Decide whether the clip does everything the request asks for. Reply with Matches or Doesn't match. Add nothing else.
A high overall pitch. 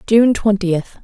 Matches